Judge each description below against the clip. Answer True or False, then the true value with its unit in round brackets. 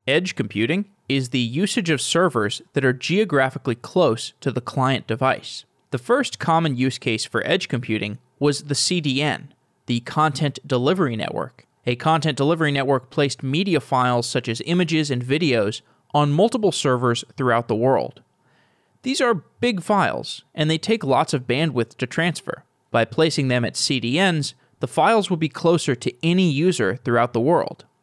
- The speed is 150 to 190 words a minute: True (165 wpm)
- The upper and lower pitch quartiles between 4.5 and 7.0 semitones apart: True (4.8 semitones)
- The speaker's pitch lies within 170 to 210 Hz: False (145 Hz)